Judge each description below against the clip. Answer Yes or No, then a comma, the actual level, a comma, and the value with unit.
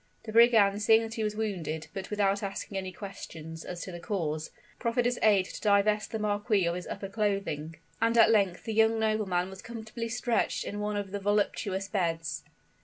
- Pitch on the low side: No, high, 205 Hz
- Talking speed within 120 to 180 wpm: No, average, 195 wpm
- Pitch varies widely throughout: No, average, 2.8 semitones